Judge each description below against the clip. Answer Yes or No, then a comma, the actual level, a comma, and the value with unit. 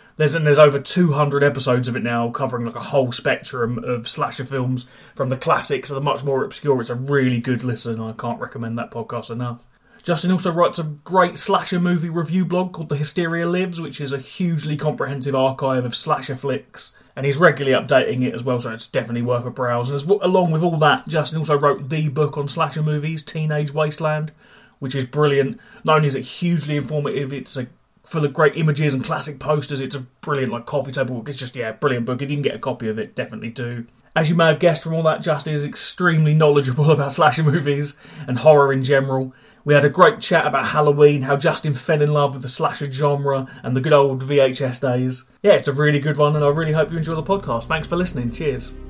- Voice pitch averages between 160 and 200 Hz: No, medium, 145 Hz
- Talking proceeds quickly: Yes, fast, 230 wpm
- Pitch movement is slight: No, average, 3.2 semitones